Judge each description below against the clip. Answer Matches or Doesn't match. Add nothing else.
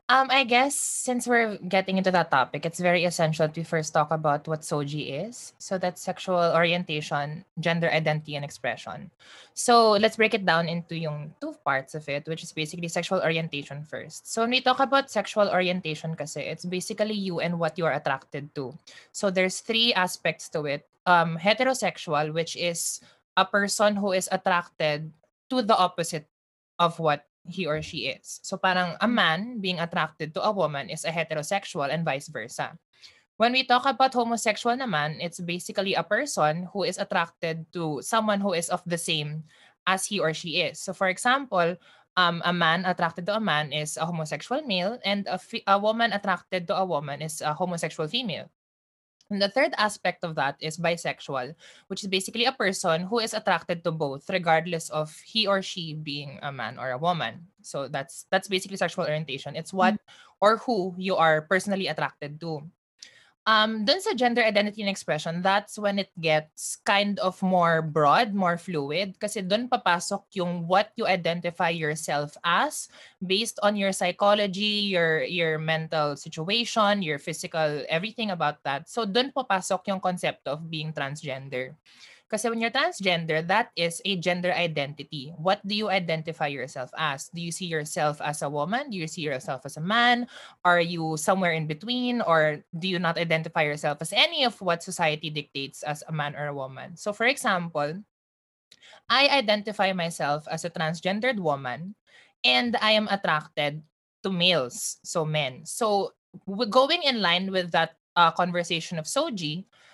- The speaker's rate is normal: Doesn't match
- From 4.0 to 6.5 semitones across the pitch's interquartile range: Matches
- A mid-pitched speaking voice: Matches